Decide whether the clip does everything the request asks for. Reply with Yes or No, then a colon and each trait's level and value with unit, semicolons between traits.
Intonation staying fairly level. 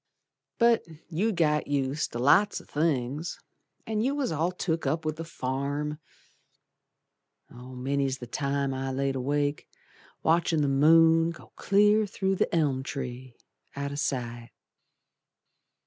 No: average, 3.7 semitones